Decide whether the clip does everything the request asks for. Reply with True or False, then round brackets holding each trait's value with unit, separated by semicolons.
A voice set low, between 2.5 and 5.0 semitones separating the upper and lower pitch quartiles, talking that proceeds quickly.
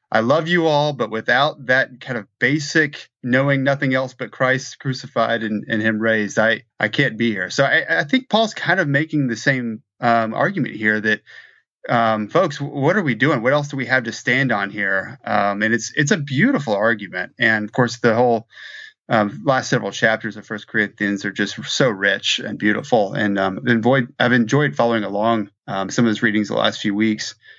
True (115 Hz; 3.8 semitones; 210 wpm)